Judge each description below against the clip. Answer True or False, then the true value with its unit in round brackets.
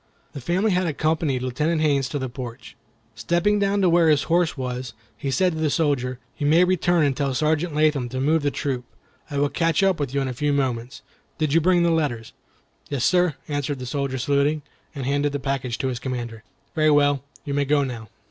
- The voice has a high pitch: False (145 Hz)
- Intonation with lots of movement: False (3.5 semitones)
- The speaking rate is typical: False (215 wpm)